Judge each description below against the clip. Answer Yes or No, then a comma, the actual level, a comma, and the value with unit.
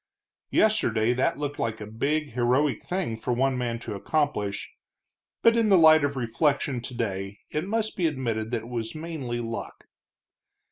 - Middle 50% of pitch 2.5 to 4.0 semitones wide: No, average, 5.2 semitones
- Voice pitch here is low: Yes, low, 125 Hz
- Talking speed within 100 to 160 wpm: No, average, 170 wpm